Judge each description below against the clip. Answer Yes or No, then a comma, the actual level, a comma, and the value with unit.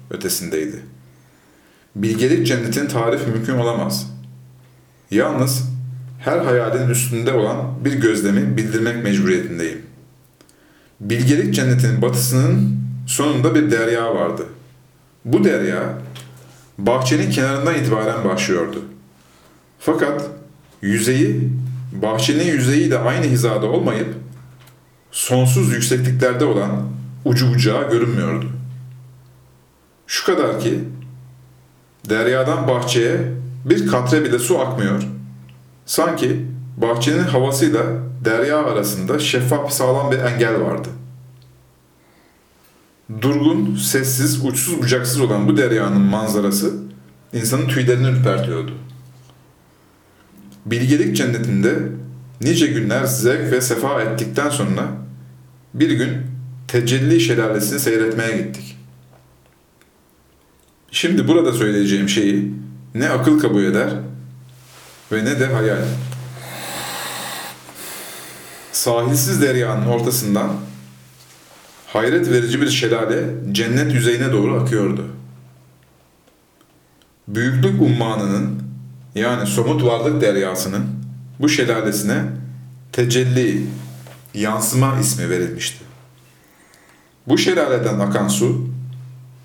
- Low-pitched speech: Yes, low, 110 Hz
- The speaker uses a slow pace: Yes, slow, 85 wpm